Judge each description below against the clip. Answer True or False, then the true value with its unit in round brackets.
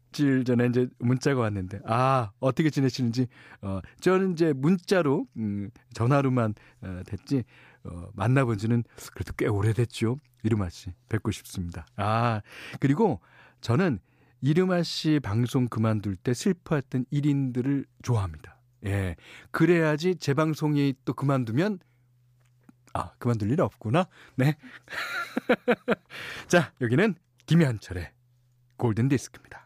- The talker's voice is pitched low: True (125 Hz)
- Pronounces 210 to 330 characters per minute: True (265 characters per minute)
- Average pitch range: True (4.7 semitones)